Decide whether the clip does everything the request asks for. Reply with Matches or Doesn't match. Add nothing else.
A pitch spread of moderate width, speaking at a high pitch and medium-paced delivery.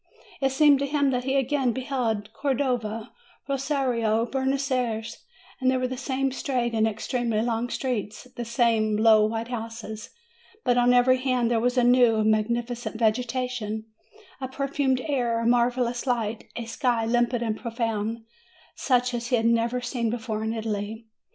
Doesn't match